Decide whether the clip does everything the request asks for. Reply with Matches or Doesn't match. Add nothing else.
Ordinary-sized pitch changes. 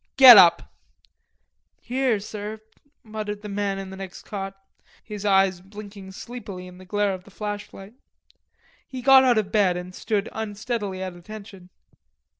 Doesn't match